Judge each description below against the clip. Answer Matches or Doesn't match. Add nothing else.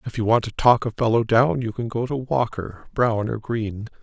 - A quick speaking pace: Matches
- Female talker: Doesn't match